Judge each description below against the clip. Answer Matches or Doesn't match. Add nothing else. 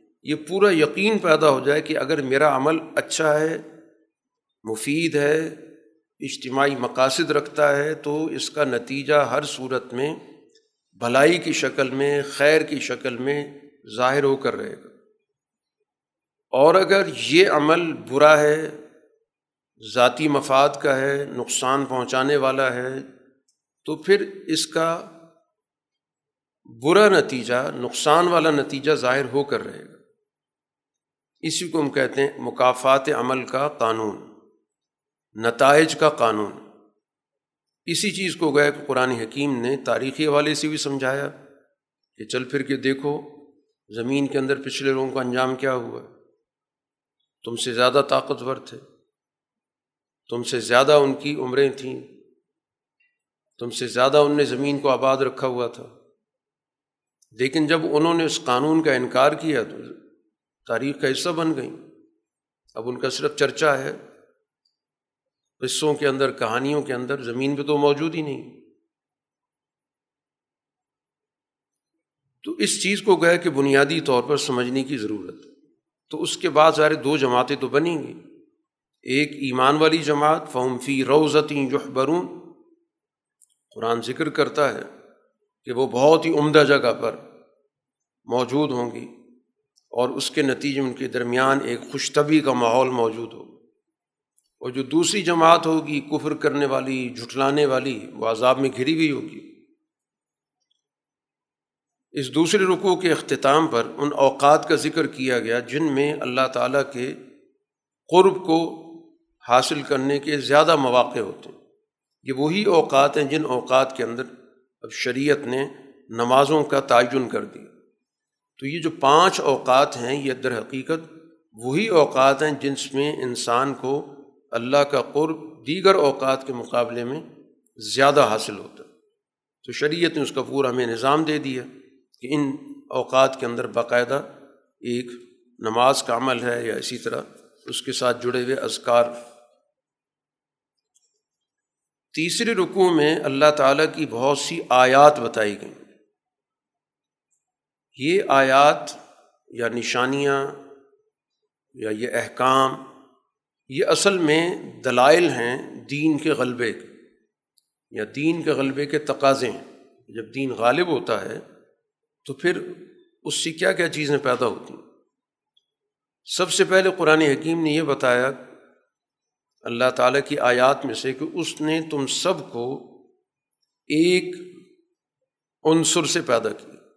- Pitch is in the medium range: Matches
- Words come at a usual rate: Matches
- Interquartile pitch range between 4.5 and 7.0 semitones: Doesn't match